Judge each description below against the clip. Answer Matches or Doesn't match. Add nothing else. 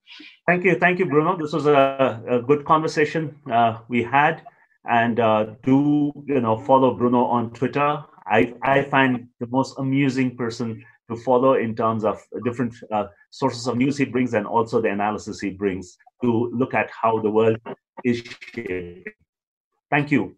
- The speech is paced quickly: Doesn't match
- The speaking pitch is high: Doesn't match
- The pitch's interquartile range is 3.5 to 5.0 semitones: Matches